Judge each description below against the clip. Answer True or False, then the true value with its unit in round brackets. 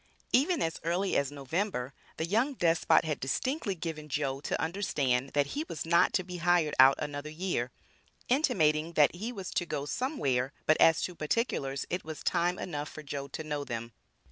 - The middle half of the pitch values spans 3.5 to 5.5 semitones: True (4.3 semitones)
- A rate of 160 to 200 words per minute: True (185 wpm)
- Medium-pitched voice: True (160 Hz)